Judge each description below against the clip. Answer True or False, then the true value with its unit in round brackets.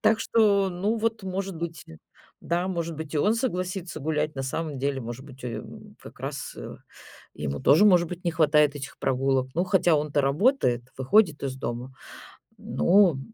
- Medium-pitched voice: True (160 Hz)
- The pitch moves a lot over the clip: True (5.8 semitones)